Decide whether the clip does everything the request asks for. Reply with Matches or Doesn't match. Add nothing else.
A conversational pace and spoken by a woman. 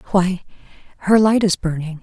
Matches